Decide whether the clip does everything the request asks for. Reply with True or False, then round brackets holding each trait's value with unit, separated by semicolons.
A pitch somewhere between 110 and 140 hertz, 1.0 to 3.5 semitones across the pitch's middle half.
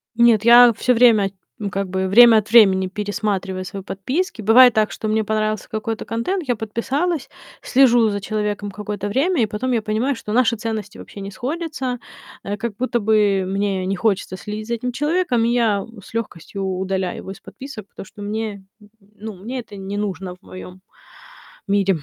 False (215 Hz; 3.2 semitones)